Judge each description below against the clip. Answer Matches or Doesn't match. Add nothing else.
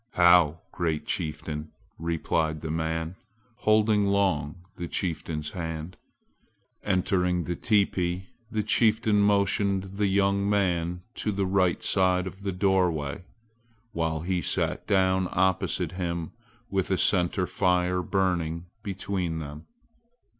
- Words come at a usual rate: Doesn't match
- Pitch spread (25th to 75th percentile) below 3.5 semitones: Matches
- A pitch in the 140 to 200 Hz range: Doesn't match